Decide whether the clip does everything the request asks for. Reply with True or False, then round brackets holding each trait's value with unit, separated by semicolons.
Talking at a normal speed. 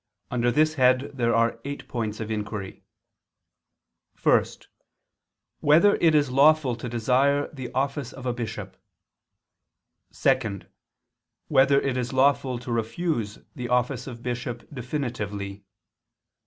False (120 wpm)